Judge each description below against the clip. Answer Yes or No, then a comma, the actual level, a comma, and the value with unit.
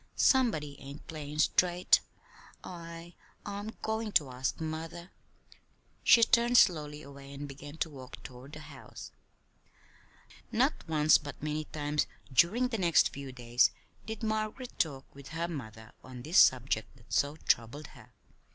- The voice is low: No, medium, 150 Hz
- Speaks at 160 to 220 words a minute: No, average, 145 wpm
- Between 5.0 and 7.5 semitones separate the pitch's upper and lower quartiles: No, average, 4.1 semitones